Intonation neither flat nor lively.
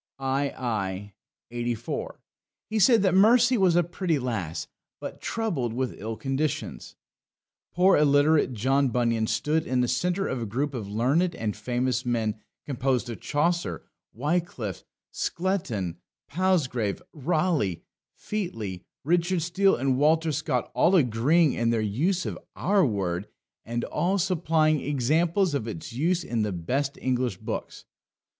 No: wide, 6.7 semitones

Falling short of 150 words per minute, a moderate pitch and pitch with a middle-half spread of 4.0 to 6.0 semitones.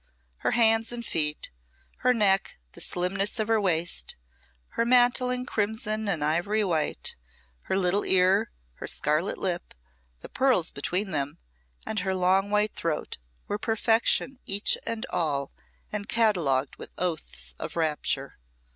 No: average, 140 wpm; high, 195 Hz; average, 4.8 semitones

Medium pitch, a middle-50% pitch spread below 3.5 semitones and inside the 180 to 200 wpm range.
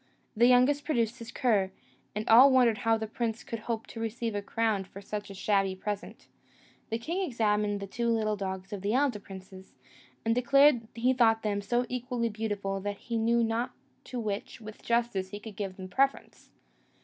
No: high, 225 Hz; average, 2.8 semitones; average, 190 wpm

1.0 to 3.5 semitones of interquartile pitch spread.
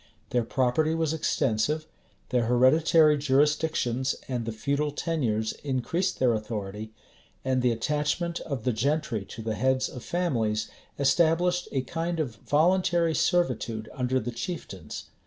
No: wide, 5.6 semitones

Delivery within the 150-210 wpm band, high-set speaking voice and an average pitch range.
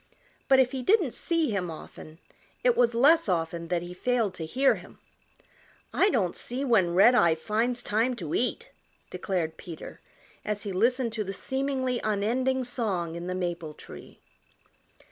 No: average, 160 wpm; high, 220 Hz; wide, 6.4 semitones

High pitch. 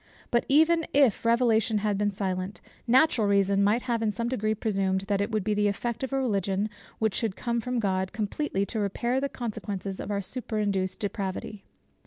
Yes: high, 210 Hz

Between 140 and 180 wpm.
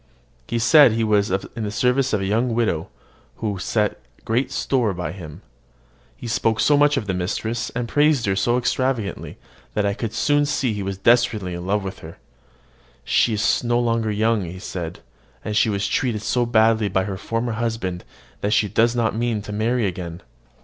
No: average, 190 wpm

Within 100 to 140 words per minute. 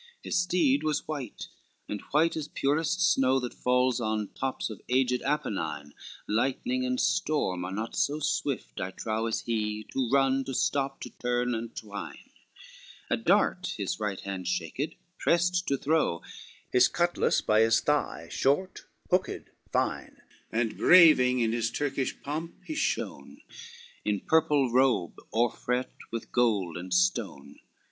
No: average, 150 wpm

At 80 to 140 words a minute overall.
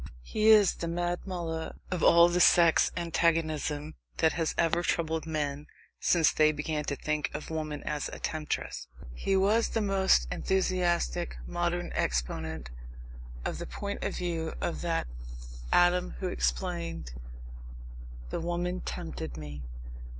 Yes: slow, 135 wpm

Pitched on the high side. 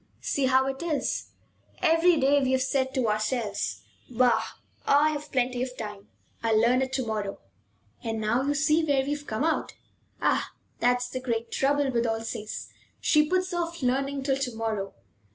Yes: very high, 260 Hz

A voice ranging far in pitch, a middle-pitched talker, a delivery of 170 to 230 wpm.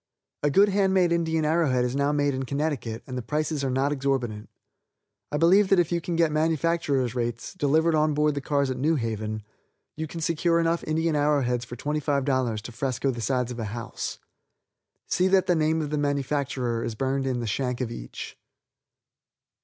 No: average, 4.2 semitones; medium, 145 Hz; average, 200 wpm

